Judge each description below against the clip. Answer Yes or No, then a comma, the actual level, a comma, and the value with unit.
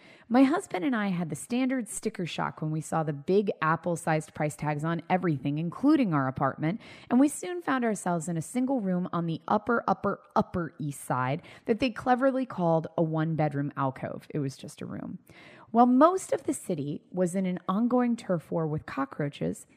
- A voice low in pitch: No, medium, 175 Hz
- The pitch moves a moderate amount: No, wide, 7.5 semitones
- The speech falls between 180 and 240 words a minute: Yes, average, 195 wpm